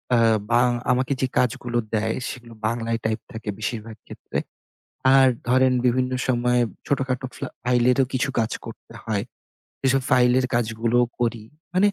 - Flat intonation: Yes, narrow, 1.9 semitones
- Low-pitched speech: Yes, low, 125 Hz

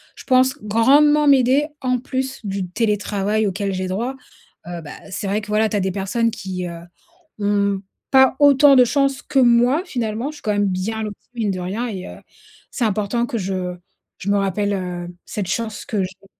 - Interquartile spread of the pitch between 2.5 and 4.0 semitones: No, average, 4.6 semitones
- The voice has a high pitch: Yes, high, 210 Hz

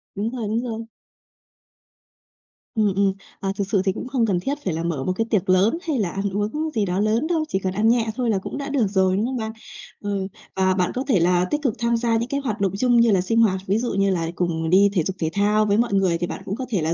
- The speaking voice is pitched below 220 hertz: Yes, high, 205 Hz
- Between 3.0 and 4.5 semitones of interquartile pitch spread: Yes, average, 3.8 semitones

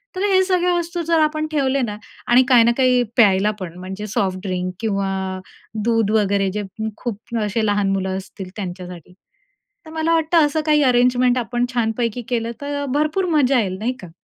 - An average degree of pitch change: No, wide, 6.3 semitones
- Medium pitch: No, high, 235 Hz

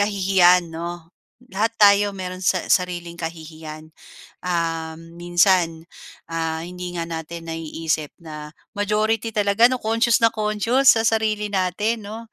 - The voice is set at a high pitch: No, medium, 180 Hz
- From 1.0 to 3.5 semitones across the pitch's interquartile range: No, average, 4.2 semitones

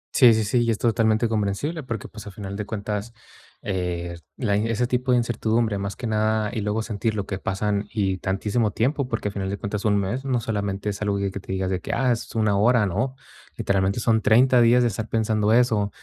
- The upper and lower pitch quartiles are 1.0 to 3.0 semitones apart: Yes, average, 2.7 semitones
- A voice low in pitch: Yes, low, 110 Hz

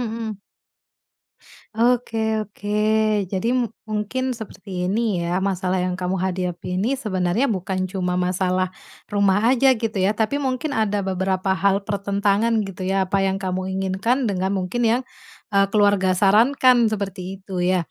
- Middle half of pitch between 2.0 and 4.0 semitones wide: Yes, average, 2.9 semitones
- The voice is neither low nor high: No, high, 200 Hz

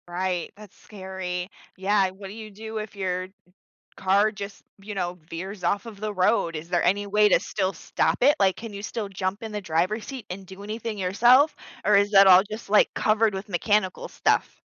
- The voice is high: Yes, high, 200 Hz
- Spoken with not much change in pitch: Yes, narrow, 2.2 semitones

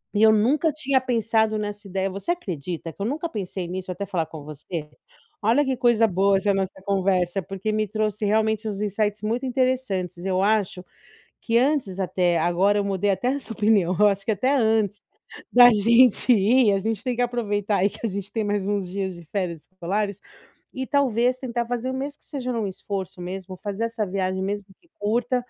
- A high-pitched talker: Yes, high, 205 Hz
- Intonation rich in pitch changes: No, average, 3.7 semitones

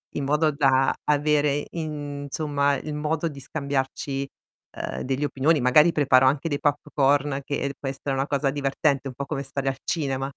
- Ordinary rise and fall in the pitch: No, narrow, 1.6 semitones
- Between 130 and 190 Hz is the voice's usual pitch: Yes, medium, 140 Hz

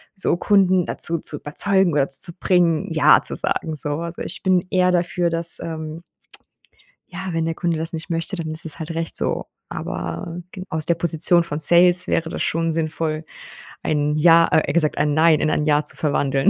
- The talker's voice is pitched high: No, medium, 165 Hz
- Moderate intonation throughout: No, narrow, 2.0 semitones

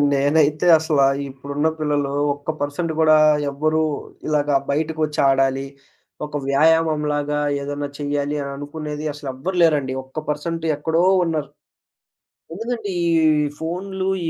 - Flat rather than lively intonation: Yes, narrow, 1.9 semitones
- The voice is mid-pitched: Yes, medium, 150 Hz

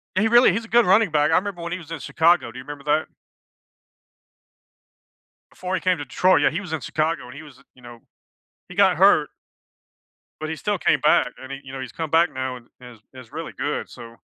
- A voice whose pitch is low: No, medium, 155 Hz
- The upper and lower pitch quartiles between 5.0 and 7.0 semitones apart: Yes, wide, 5.5 semitones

